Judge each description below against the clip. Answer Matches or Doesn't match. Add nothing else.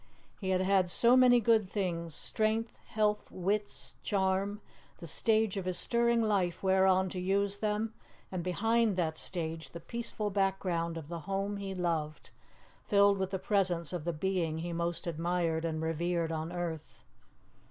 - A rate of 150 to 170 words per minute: Matches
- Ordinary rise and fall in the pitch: Matches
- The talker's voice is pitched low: Doesn't match